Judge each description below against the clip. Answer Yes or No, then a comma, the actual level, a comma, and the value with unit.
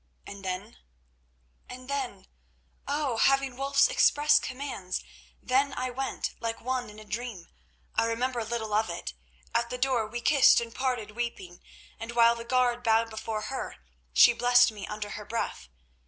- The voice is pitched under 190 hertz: No, high, 235 Hz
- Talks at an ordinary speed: Yes, average, 155 wpm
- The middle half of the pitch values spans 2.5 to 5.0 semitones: Yes, average, 3.0 semitones